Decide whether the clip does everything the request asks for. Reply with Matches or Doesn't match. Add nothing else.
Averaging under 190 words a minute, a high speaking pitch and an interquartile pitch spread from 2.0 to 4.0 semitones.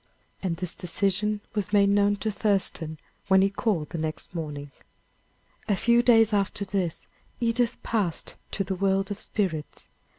Matches